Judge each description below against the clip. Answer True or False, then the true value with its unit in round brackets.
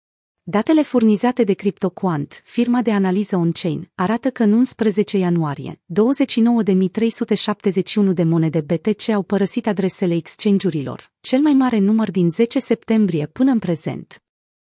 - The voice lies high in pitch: True (205 Hz)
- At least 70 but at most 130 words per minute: True (125 wpm)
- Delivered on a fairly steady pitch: False (4.2 semitones)